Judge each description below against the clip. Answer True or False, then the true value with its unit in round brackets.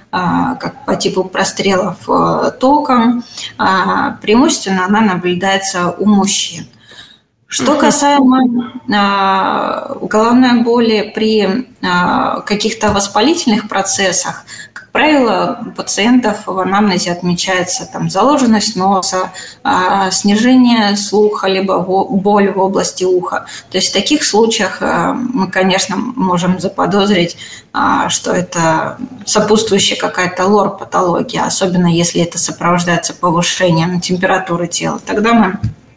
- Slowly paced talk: True (100 wpm)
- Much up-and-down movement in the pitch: False (4.2 semitones)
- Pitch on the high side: True (200 Hz)